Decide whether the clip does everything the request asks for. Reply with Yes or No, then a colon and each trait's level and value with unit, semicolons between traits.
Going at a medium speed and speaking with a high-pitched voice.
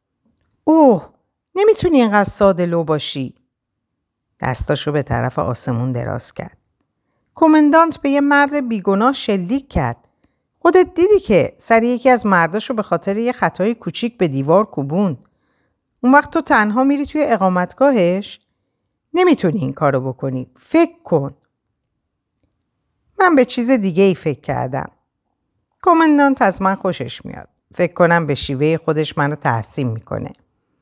Yes: average, 130 wpm; high, 195 Hz